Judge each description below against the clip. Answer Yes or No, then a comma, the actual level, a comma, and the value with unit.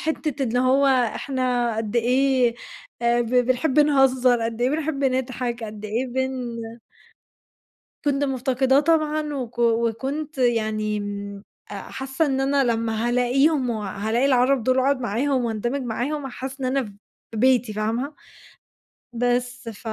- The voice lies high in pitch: Yes, very high, 250 Hz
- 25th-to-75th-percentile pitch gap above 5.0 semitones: No, narrow, 2.6 semitones